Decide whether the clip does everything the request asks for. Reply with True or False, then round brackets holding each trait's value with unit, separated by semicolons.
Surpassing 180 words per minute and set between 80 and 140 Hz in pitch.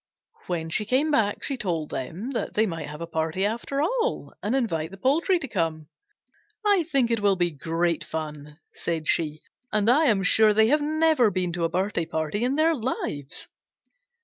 False (190 wpm; 205 Hz)